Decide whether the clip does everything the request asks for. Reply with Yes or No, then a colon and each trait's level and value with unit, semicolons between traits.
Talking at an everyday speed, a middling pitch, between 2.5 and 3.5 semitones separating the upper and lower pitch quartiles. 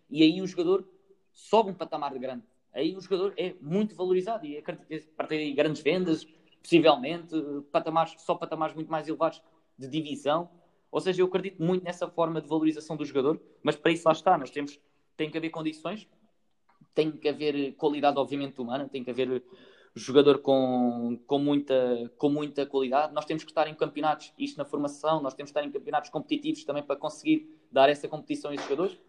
No: fast, 190 wpm; medium, 155 Hz; average, 2.9 semitones